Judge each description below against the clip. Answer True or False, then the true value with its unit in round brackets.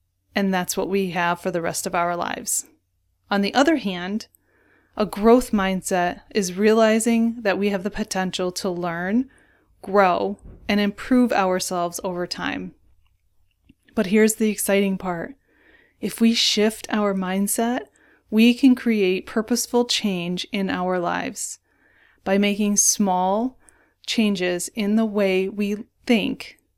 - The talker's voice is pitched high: True (200 Hz)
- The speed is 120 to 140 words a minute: True (135 wpm)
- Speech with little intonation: False (3.3 semitones)